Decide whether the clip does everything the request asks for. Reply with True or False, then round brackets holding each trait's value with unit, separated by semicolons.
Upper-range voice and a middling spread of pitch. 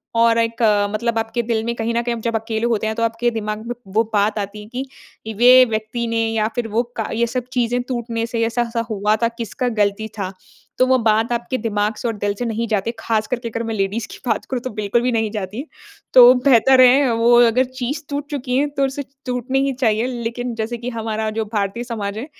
False (230 Hz; 2.0 semitones)